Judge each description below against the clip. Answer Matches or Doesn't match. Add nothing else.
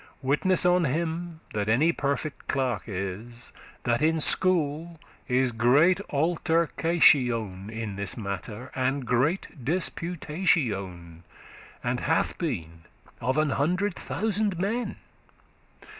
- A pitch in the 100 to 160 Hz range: Matches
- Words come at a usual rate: Doesn't match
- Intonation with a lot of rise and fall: Matches